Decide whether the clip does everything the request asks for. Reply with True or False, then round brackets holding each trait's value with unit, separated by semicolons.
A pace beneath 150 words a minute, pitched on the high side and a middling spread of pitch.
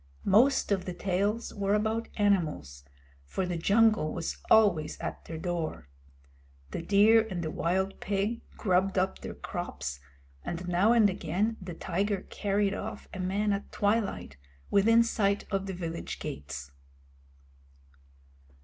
True (140 wpm; 195 Hz; 3.3 semitones)